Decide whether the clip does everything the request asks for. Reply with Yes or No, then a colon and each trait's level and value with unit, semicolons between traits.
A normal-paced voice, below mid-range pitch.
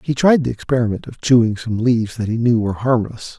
No: fast, 230 wpm; low, 120 Hz